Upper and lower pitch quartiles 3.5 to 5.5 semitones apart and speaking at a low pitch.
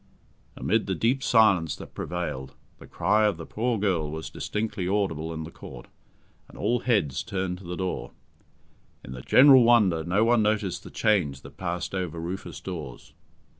Yes: average, 4.7 semitones; very low, 95 Hz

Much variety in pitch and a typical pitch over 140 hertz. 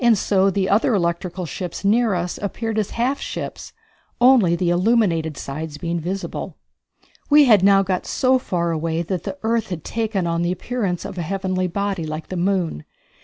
No: average, 3.5 semitones; medium, 185 Hz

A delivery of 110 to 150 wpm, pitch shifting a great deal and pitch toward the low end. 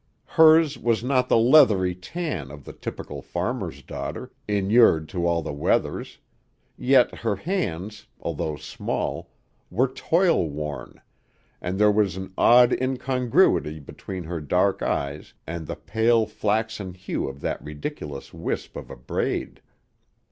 Yes: slow, 135 wpm; wide, 7.1 semitones; low, 100 Hz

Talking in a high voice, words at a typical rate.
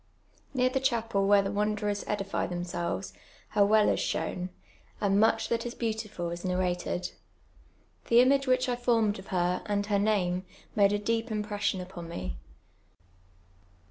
Yes: high, 205 Hz; average, 160 wpm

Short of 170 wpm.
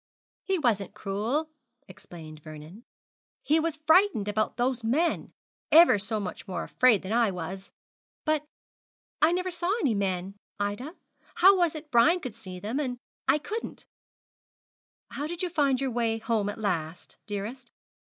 Yes: average, 155 wpm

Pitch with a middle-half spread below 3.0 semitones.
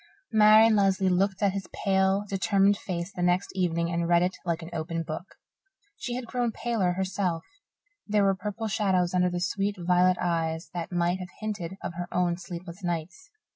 Yes: narrow, 2.4 semitones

